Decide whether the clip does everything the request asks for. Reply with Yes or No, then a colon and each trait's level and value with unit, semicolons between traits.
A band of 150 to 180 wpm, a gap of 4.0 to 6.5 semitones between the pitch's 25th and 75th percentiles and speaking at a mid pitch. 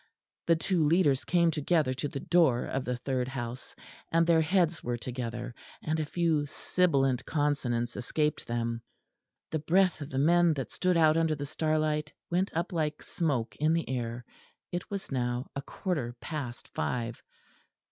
Yes: average, 165 wpm; average, 4.8 semitones; medium, 150 Hz